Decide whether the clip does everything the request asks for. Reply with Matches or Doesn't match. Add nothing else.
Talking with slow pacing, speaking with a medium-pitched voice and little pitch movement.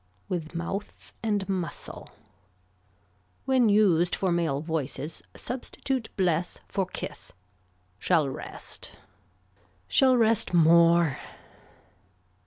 Doesn't match